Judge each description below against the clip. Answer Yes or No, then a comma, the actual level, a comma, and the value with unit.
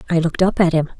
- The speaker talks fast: Yes, fast, 300 wpm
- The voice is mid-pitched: Yes, medium, 170 Hz